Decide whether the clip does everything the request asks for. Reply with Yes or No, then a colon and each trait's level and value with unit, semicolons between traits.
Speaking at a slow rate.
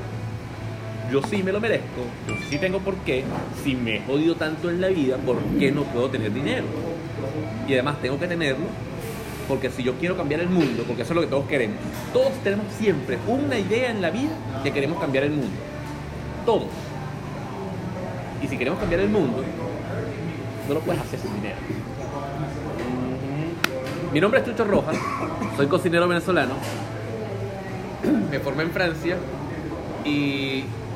No: average, 160 wpm